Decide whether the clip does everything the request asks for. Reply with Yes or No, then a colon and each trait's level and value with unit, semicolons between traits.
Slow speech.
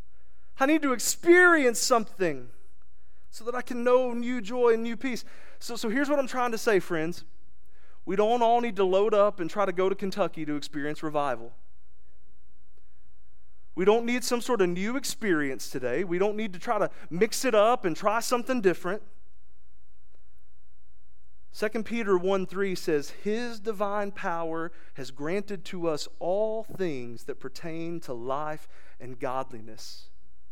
No: average, 160 wpm